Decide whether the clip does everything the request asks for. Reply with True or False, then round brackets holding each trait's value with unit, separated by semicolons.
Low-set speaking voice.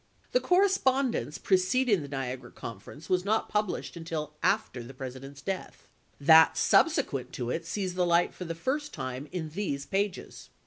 False (170 Hz)